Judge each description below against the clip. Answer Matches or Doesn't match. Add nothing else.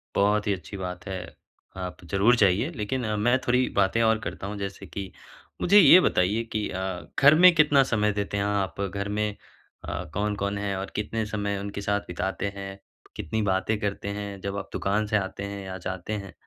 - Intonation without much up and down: Matches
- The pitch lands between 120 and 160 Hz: Doesn't match